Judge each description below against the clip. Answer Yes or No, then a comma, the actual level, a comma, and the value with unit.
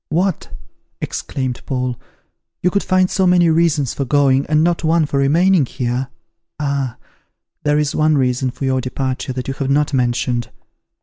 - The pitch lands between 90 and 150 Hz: Yes, medium, 140 Hz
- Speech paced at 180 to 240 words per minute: No, average, 165 wpm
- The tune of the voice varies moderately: Yes, average, 3.7 semitones